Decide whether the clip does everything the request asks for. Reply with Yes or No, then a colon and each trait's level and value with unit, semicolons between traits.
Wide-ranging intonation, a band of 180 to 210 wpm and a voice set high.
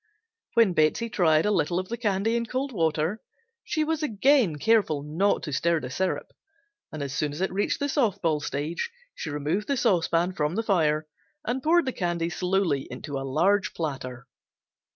No: wide, 6.5 semitones; average, 185 wpm; medium, 180 Hz